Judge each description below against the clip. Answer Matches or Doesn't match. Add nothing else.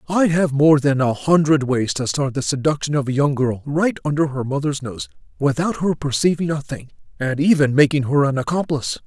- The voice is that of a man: Matches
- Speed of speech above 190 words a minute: Matches